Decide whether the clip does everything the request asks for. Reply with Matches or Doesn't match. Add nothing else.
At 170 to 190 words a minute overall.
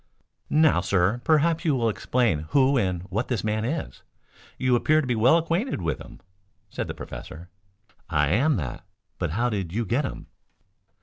Matches